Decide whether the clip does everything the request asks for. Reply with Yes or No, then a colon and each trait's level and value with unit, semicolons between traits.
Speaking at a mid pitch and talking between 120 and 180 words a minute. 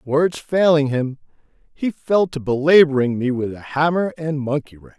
Yes: medium, 145 Hz; average, 170 wpm